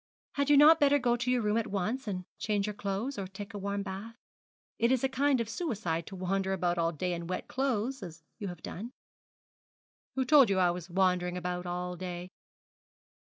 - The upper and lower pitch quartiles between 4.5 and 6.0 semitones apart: Yes, average, 5.3 semitones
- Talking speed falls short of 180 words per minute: No, fast, 205 wpm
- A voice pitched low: No, high, 200 Hz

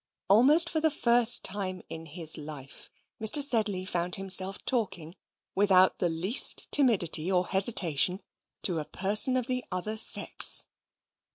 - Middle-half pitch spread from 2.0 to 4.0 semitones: No, average, 5.1 semitones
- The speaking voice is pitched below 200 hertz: Yes, high, 190 Hz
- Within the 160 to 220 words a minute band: No, average, 140 wpm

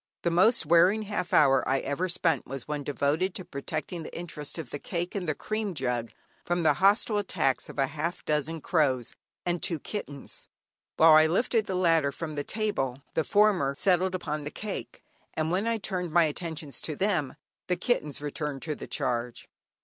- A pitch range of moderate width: Yes, average, 4.3 semitones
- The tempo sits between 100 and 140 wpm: No, average, 190 wpm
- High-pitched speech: No, medium, 165 Hz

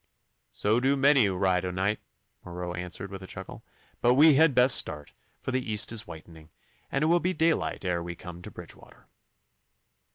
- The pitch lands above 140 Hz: No, low, 100 Hz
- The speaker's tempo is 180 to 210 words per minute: Yes, average, 190 wpm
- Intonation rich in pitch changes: Yes, wide, 7.0 semitones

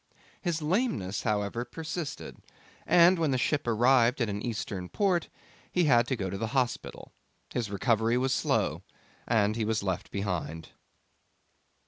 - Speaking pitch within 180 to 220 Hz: No, low, 120 Hz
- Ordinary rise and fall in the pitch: No, wide, 6.0 semitones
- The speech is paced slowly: No, average, 145 wpm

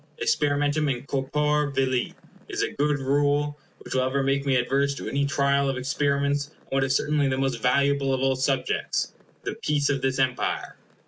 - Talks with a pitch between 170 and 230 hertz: No, medium, 140 Hz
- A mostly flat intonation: Yes, narrow, 1.4 semitones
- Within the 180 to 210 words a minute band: Yes, average, 185 wpm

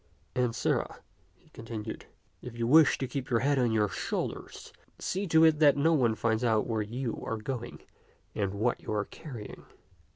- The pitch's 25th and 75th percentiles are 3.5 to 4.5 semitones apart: Yes, average, 4.1 semitones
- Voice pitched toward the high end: No, low, 120 Hz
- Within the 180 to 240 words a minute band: Yes, average, 190 wpm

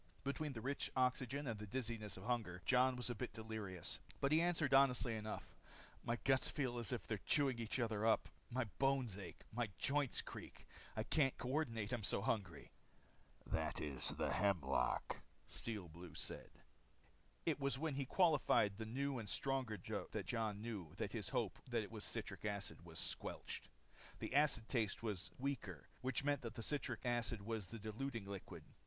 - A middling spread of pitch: Yes, average, 4.4 semitones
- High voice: No, low, 115 Hz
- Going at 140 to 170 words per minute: No, average, 180 wpm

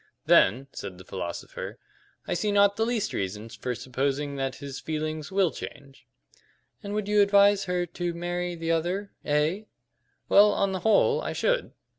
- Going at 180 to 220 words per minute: No, average, 165 wpm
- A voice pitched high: No, medium, 175 Hz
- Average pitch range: No, wide, 6.4 semitones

